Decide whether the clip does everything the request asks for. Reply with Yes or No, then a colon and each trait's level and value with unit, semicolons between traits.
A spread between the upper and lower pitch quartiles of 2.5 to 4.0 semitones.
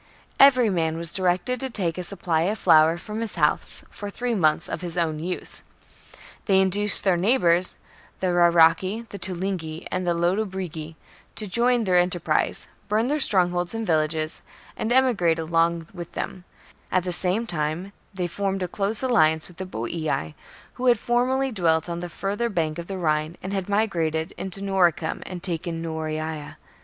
Yes: average, 3.6 semitones